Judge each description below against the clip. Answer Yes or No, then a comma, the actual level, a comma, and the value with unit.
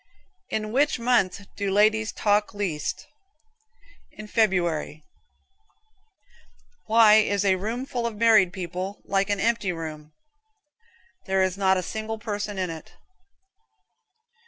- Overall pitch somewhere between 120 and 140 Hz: No, high, 205 Hz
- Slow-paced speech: Yes, slow, 120 wpm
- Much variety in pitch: No, average, 2.8 semitones